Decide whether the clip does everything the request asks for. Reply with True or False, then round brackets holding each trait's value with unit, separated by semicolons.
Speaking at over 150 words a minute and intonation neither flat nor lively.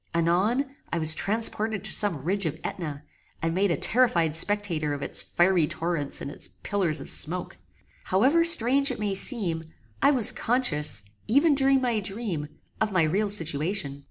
False (165 wpm; 5.9 semitones)